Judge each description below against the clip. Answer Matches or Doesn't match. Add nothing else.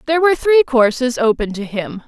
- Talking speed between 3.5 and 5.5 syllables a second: Doesn't match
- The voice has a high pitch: Matches